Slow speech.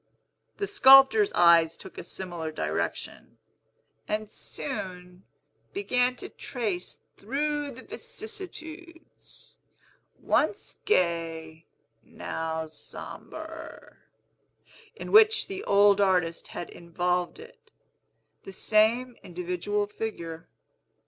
Yes: slow, 90 wpm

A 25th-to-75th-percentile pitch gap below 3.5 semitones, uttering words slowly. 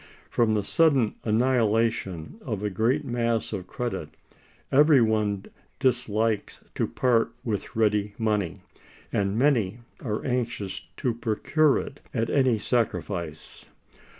Yes: average, 3.1 semitones; slow, 120 wpm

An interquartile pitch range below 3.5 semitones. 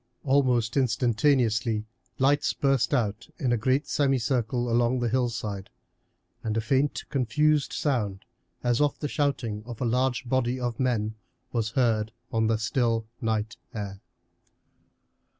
Yes: average, 3.0 semitones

